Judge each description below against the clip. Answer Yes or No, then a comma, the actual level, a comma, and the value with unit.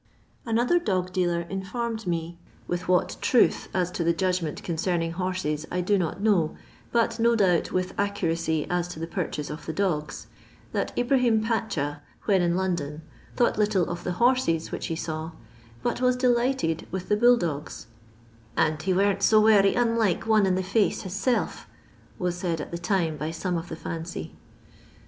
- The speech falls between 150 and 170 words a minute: No, average, 180 wpm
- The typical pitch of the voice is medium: Yes, medium, 180 Hz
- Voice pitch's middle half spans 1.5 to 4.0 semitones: No, average, 4.4 semitones